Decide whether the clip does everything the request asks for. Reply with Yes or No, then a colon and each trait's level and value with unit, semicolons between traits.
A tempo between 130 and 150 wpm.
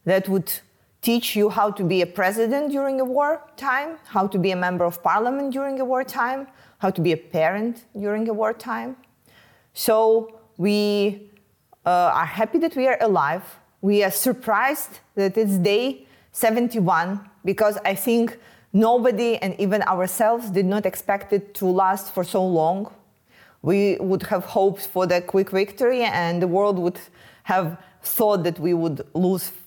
No: average, 165 wpm